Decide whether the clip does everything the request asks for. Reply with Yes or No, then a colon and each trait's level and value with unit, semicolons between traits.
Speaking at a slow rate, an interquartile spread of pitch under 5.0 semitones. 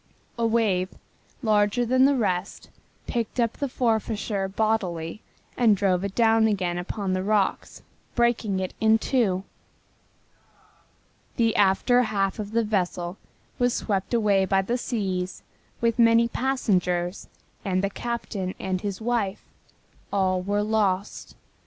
Yes: slow, 130 wpm; average, 3.4 semitones